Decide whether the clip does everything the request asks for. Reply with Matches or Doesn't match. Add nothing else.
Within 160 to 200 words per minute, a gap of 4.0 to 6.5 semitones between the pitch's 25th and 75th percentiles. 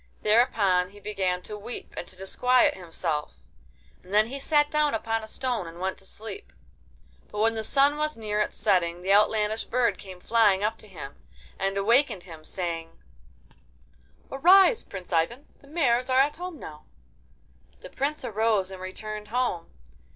Matches